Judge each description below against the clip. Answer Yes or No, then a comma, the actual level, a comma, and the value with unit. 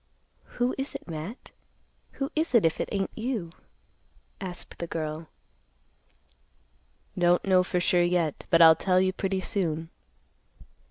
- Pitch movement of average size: Yes, average, 3.2 semitones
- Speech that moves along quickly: No, average, 140 wpm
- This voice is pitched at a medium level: Yes, medium, 180 Hz